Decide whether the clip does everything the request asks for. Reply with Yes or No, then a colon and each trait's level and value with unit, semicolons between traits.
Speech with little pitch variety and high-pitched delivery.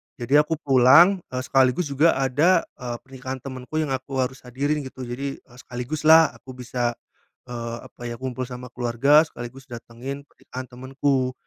No: narrow, 2.3 semitones; low, 130 Hz